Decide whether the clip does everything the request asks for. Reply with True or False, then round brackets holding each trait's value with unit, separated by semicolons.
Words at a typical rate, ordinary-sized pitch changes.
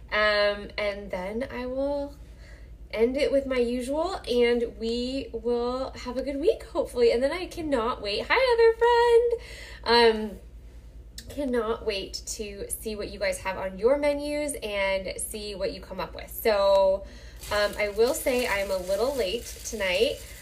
False (160 wpm; 6.0 semitones)